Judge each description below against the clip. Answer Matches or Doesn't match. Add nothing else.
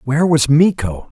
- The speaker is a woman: Doesn't match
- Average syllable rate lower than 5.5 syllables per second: Matches